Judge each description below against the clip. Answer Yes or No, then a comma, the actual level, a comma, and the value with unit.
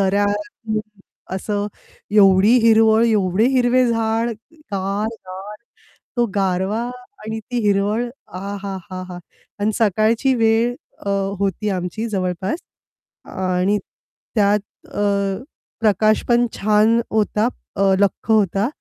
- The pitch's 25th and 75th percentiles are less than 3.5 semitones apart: Yes, narrow, 2.4 semitones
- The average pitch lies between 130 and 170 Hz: No, high, 210 Hz